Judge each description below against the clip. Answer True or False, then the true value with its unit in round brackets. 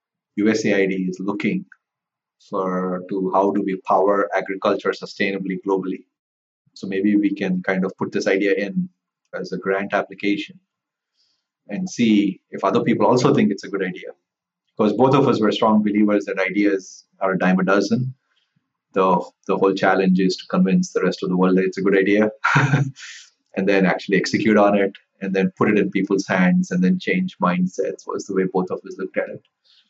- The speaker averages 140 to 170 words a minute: False (190 wpm)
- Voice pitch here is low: True (100 Hz)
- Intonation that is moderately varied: False (2.2 semitones)